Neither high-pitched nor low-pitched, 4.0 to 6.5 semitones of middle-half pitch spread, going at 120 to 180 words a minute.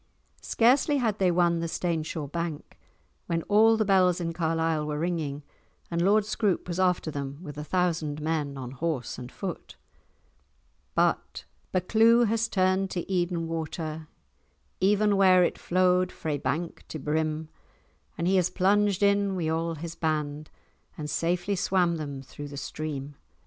No: medium, 170 Hz; average, 3.5 semitones; average, 155 wpm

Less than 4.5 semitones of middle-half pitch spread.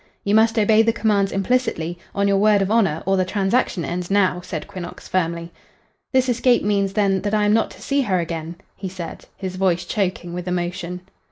Yes: average, 2.9 semitones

